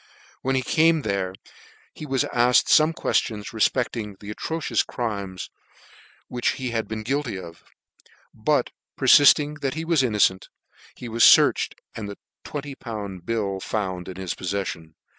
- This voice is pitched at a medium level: No, low, 115 Hz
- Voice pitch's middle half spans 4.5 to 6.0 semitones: Yes, average, 5.2 semitones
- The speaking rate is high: No, average, 145 wpm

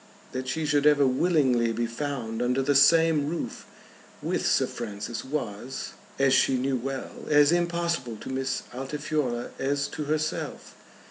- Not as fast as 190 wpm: Yes, average, 145 wpm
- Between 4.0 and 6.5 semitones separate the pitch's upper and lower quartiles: No, average, 3.2 semitones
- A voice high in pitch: No, low, 135 Hz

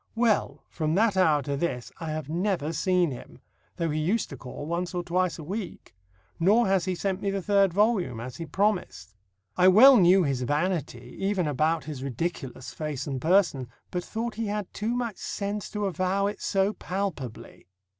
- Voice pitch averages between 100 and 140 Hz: No, medium, 180 Hz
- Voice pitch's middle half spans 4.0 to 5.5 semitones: Yes, average, 4.7 semitones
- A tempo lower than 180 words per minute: No, average, 185 wpm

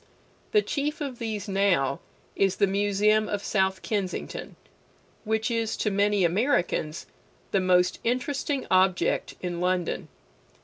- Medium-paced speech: No, slow, 125 wpm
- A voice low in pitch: No, high, 200 Hz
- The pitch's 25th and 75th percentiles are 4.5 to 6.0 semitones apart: No, average, 3.4 semitones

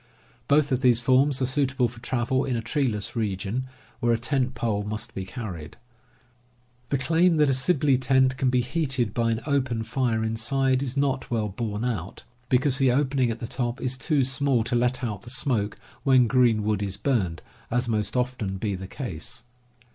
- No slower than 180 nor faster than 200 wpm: Yes, average, 190 wpm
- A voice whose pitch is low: Yes, low, 125 Hz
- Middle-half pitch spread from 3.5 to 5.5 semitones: No, average, 3.1 semitones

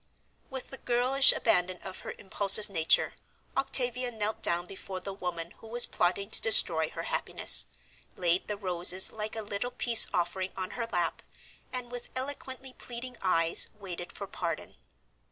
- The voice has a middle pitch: No, high, 200 Hz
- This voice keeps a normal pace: Yes, average, 155 wpm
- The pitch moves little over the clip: No, average, 5.1 semitones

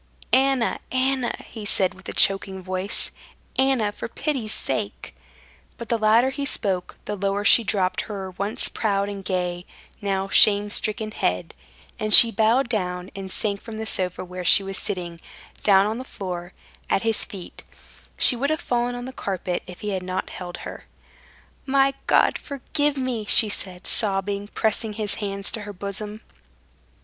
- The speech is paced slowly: No, average, 170 wpm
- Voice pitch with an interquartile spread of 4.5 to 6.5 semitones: No, average, 3.5 semitones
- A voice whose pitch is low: No, high, 205 Hz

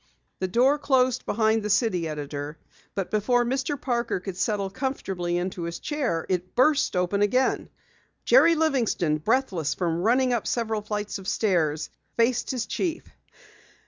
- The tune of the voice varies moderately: No, wide, 6.0 semitones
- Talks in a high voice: Yes, high, 215 Hz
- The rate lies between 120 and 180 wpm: Yes, average, 145 wpm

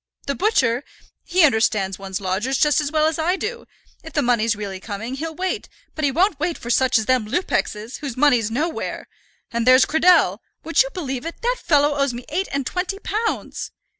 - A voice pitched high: Yes, very high, 280 Hz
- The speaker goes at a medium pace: Yes, average, 195 wpm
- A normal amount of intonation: No, wide, 6.3 semitones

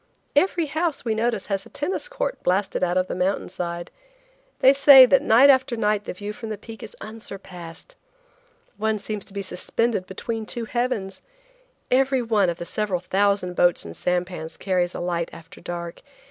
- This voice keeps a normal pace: Yes, average, 175 wpm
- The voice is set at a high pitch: Yes, high, 210 Hz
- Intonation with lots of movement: No, average, 5.0 semitones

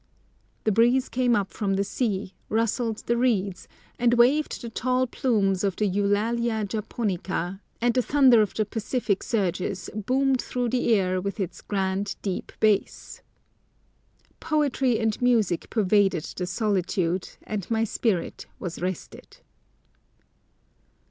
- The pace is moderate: No, slow, 130 wpm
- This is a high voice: Yes, high, 215 Hz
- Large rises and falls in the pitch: No, average, 3.7 semitones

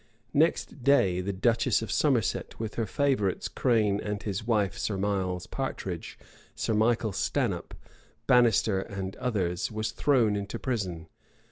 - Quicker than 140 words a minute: No, slow, 135 wpm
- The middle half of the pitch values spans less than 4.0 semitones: Yes, average, 3.6 semitones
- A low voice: Yes, low, 105 Hz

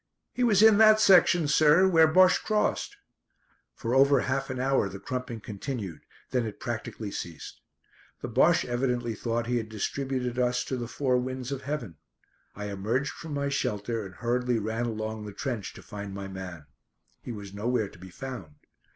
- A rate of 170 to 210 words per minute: Yes, average, 175 wpm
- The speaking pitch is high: No, low, 120 Hz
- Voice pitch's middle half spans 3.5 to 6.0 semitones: Yes, average, 4.5 semitones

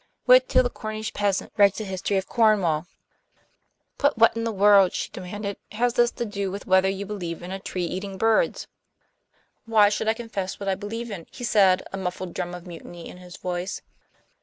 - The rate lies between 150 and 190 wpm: No, average, 200 wpm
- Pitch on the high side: Yes, high, 200 Hz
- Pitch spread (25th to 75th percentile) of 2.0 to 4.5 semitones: Yes, average, 3.1 semitones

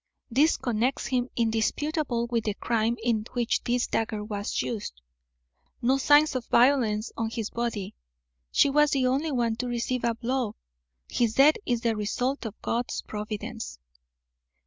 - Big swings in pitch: No, average, 2.7 semitones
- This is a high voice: Yes, high, 235 Hz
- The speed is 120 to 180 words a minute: Yes, average, 150 wpm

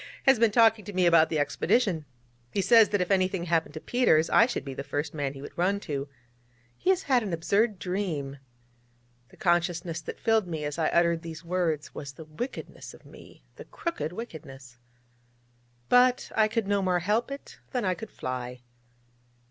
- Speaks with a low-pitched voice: No, medium, 175 Hz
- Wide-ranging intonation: Yes, wide, 5.8 semitones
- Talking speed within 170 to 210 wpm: Yes, average, 190 wpm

